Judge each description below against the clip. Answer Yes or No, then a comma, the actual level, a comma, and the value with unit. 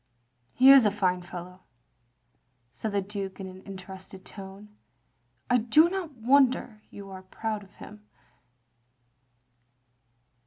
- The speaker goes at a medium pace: No, slow, 130 wpm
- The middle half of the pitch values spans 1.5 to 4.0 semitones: Yes, average, 3.1 semitones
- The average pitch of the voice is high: Yes, high, 200 Hz